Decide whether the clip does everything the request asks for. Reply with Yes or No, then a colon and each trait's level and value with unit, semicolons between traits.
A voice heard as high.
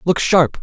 No: medium, 165 Hz